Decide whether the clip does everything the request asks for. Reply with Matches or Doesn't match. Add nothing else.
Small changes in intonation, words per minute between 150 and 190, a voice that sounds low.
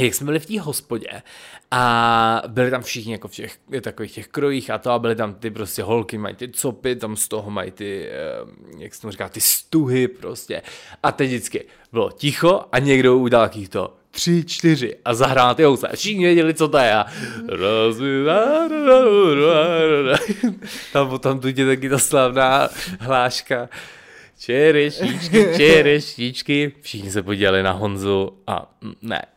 Doesn't match